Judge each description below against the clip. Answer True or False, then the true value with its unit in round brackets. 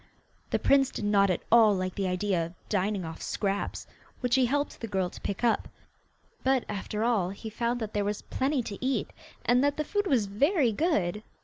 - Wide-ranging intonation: False (4.7 semitones)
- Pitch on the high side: True (215 Hz)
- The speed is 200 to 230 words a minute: True (205 wpm)